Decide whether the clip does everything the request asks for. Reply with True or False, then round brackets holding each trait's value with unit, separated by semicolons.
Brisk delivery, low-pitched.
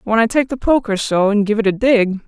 False (240 wpm; 220 Hz)